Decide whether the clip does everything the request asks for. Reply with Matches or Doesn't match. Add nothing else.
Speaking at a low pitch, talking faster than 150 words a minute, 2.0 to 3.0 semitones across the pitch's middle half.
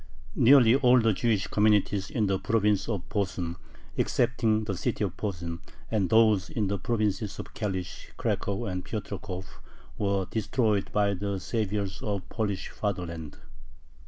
Doesn't match